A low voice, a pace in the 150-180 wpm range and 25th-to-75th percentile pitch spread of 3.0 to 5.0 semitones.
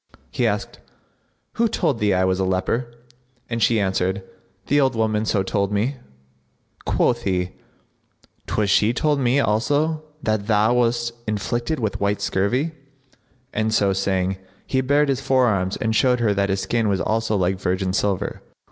Yes: low, 110 Hz; average, 160 wpm; average, 3.9 semitones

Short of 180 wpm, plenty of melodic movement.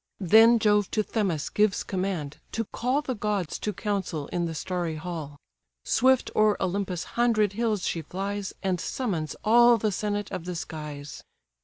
No: average, 160 wpm; average, 3.9 semitones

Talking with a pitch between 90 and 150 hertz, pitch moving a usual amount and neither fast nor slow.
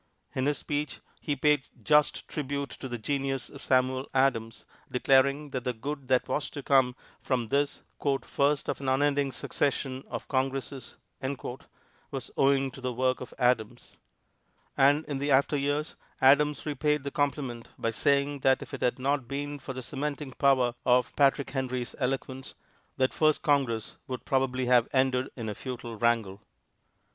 No: low, 135 Hz; narrow, 2.1 semitones; average, 160 wpm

